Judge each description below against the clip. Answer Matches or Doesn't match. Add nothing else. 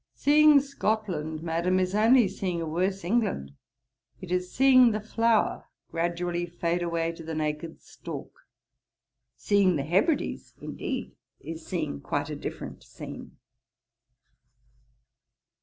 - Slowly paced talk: Matches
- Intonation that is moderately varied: Matches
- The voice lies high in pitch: Doesn't match